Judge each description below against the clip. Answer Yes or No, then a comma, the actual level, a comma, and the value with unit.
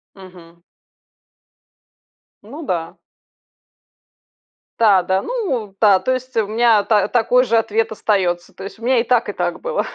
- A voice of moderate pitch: No, high, 220 Hz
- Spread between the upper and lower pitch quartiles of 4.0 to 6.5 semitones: Yes, average, 4.3 semitones